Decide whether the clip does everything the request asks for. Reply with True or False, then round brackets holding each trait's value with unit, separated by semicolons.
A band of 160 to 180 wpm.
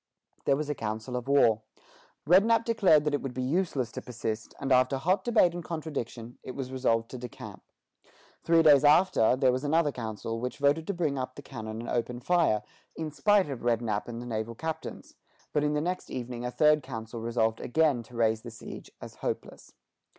False (200 wpm)